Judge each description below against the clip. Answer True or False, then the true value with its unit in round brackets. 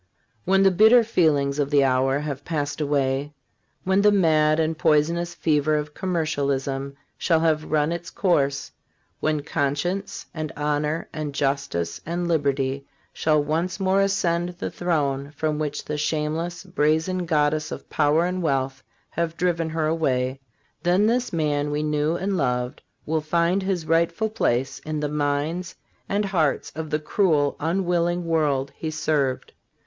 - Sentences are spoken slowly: False (155 wpm)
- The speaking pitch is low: False (155 Hz)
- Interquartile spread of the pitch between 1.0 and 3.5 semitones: True (3.1 semitones)